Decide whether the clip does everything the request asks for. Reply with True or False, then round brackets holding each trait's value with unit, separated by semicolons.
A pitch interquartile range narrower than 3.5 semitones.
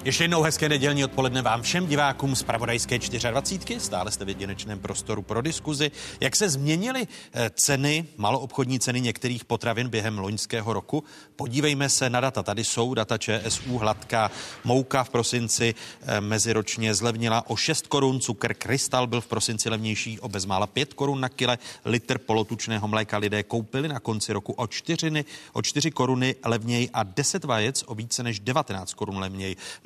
False (3.8 semitones)